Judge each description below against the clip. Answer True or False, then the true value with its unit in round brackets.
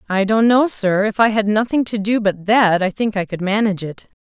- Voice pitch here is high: True (210 Hz)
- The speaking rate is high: True (255 wpm)